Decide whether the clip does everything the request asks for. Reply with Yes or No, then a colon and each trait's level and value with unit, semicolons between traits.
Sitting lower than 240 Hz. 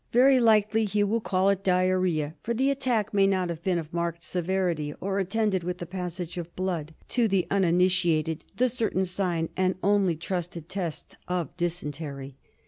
Yes: medium, 185 Hz